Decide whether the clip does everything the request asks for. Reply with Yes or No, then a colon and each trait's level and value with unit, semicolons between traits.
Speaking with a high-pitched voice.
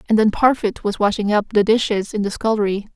Yes: high, 210 Hz